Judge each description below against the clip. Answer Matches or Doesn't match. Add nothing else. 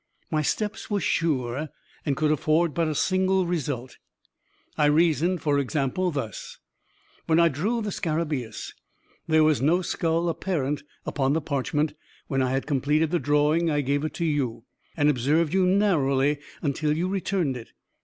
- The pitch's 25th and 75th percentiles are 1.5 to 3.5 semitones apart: Matches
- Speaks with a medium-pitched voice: Matches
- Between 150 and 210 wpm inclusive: Matches